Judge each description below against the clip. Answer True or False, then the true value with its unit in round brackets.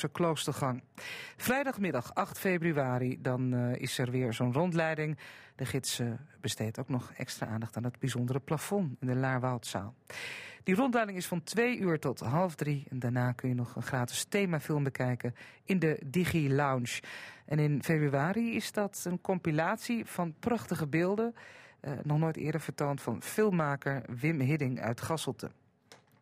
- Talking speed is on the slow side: False (160 wpm)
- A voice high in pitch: False (150 Hz)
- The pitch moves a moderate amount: False (5.8 semitones)